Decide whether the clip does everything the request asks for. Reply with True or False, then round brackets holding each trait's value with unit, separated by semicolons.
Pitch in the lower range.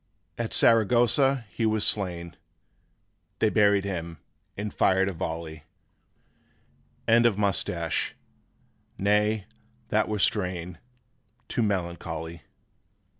True (100 Hz)